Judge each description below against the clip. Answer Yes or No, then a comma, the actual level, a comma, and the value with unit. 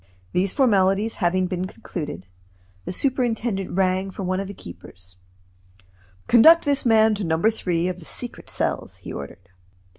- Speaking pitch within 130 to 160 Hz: No, high, 190 Hz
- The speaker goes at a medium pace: Yes, average, 150 wpm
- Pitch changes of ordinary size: Yes, average, 4.0 semitones